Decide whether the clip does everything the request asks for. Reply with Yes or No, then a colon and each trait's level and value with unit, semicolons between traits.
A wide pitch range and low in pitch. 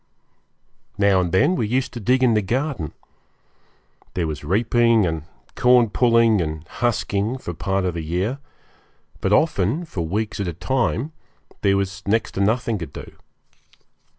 No: average, 4.7 semitones; low, 105 Hz